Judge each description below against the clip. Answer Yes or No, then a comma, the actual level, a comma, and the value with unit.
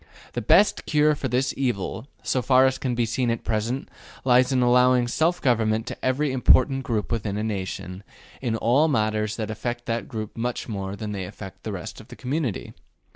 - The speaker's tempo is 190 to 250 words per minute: Yes, average, 195 wpm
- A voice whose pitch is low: Yes, low, 120 Hz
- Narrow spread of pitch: No, average, 3.3 semitones